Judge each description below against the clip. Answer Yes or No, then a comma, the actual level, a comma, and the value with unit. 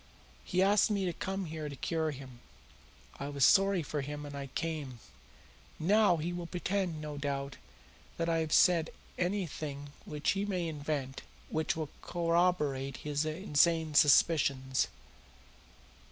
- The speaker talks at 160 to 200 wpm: No, average, 140 wpm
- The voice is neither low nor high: Yes, medium, 155 Hz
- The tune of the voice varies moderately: Yes, average, 3.6 semitones